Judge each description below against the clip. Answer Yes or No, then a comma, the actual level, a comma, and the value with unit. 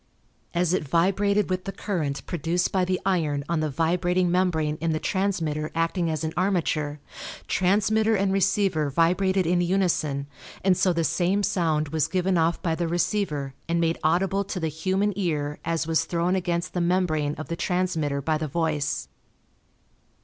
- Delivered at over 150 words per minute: Yes, average, 170 wpm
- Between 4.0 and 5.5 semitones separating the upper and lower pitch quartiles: No, average, 3.0 semitones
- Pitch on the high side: No, medium, 170 Hz